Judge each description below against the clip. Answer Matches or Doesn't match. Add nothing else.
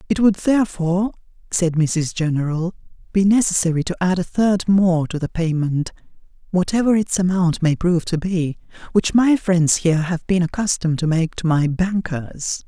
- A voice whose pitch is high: Doesn't match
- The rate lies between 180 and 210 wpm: Doesn't match